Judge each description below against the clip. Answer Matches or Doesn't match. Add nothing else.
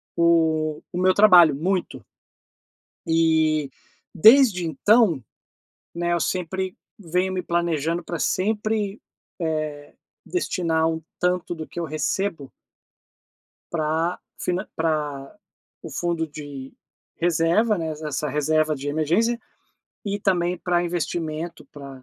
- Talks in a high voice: Doesn't match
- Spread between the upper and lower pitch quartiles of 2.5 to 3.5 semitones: Matches